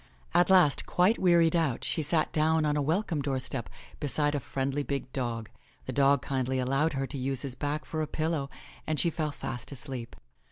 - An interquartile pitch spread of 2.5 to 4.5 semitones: Yes, average, 2.9 semitones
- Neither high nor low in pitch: Yes, medium, 145 Hz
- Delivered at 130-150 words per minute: No, average, 195 wpm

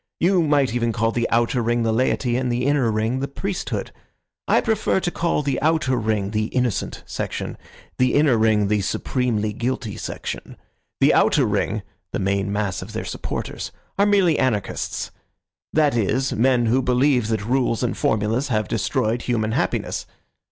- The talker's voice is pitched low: Yes, low, 120 Hz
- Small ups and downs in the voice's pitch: No, average, 3.7 semitones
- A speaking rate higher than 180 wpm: No, average, 160 wpm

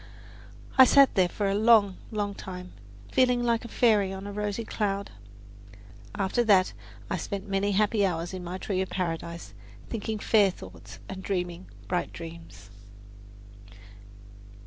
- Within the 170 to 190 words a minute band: No, average, 145 wpm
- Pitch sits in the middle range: No, high, 195 Hz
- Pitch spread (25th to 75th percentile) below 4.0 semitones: Yes, average, 2.8 semitones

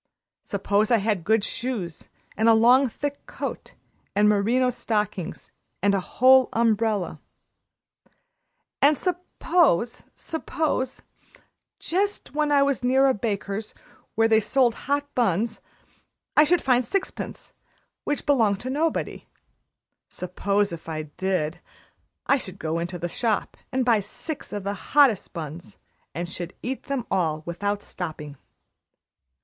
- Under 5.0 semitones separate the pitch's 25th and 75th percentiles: No, wide, 5.5 semitones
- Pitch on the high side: Yes, high, 220 Hz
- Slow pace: Yes, slow, 130 wpm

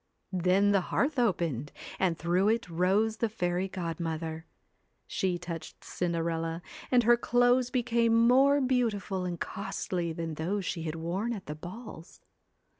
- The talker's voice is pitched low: No, medium, 185 Hz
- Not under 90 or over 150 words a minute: Yes, average, 140 wpm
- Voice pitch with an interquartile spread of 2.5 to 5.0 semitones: No, wide, 5.4 semitones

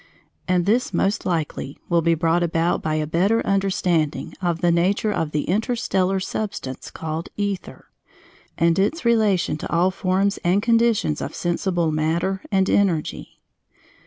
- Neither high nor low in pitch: Yes, medium, 180 Hz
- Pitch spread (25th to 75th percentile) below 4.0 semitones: Yes, average, 3.3 semitones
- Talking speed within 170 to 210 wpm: No, average, 145 wpm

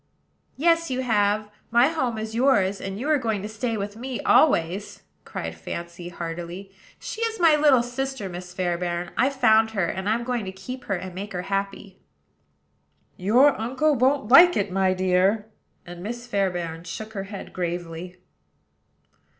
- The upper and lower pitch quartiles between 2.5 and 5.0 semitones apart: No, wide, 5.4 semitones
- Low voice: No, high, 205 Hz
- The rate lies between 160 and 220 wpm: Yes, average, 165 wpm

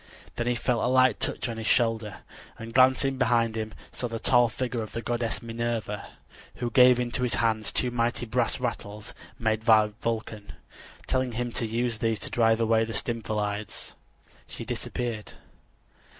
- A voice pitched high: No, low, 115 Hz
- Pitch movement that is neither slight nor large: No, narrow, 1.7 semitones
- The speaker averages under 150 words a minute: No, average, 165 wpm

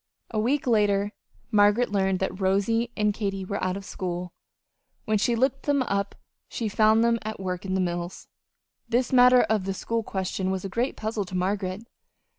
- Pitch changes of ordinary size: Yes, average, 3.2 semitones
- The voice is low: No, high, 205 Hz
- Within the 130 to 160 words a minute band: No, average, 185 wpm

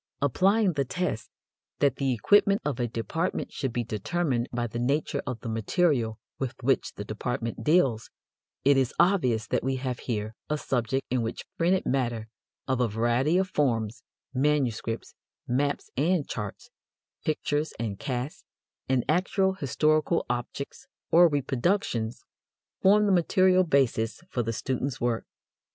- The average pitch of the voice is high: No, low, 130 Hz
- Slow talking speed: No, average, 145 wpm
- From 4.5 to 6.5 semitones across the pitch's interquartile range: Yes, average, 5.1 semitones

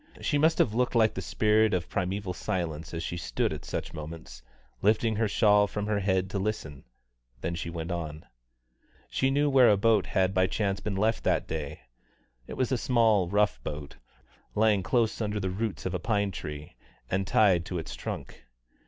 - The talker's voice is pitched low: Yes, low, 100 Hz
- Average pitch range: Yes, average, 4.2 semitones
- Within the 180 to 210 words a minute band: Yes, average, 190 wpm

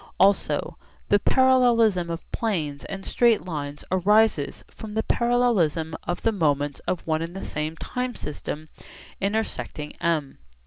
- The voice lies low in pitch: No, medium, 185 Hz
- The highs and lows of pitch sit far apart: Yes, wide, 6.1 semitones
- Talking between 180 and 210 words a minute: No, slow, 135 wpm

